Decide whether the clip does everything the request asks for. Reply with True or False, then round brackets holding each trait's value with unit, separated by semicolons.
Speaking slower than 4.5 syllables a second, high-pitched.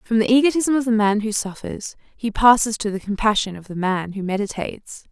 False (5.6 syllables/s; 215 Hz)